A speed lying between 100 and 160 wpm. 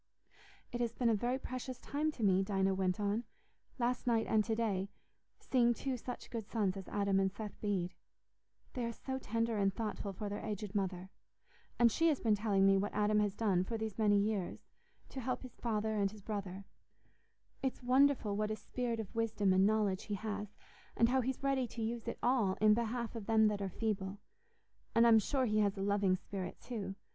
No: fast, 205 wpm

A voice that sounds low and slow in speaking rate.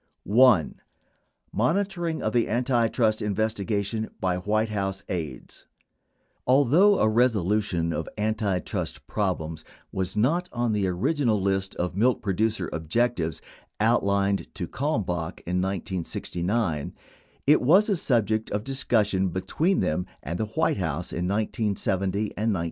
Yes: low, 105 Hz; slow, 125 wpm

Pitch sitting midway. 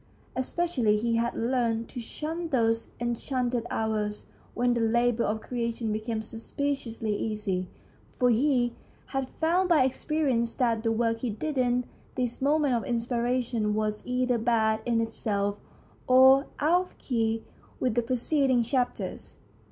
No: high, 240 Hz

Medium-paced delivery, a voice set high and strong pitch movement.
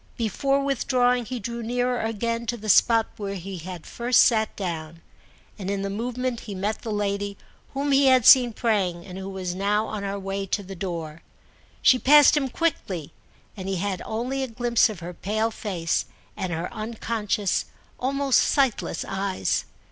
No: average, 175 wpm; high, 215 Hz; average, 4.1 semitones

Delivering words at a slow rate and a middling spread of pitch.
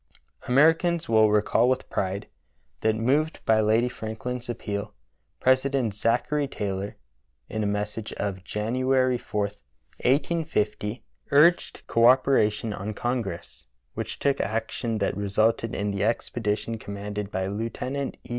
Yes: slow, 130 wpm; average, 3.8 semitones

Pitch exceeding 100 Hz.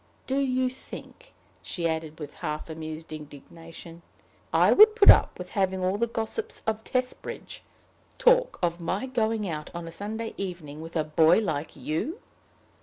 Yes: medium, 185 Hz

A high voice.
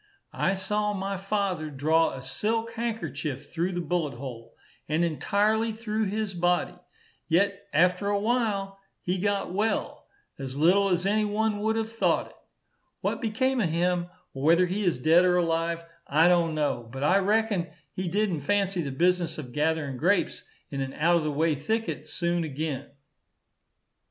No: medium, 180 Hz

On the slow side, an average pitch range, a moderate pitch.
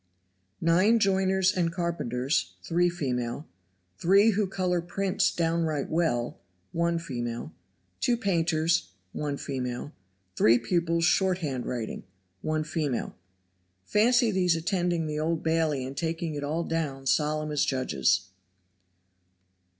Yes: slow, 115 wpm; average, 4.1 semitones; medium, 165 Hz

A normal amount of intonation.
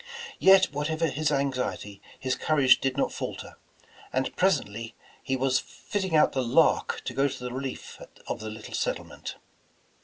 Yes: average, 3.2 semitones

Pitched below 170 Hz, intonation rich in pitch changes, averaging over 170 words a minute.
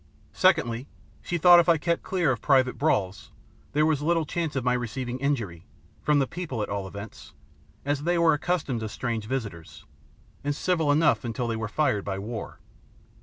Yes: low, 135 Hz; wide, 6.0 semitones; average, 180 wpm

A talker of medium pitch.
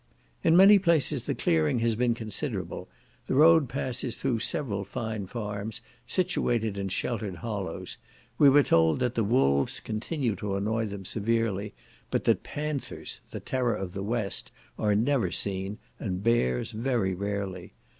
No: low, 110 Hz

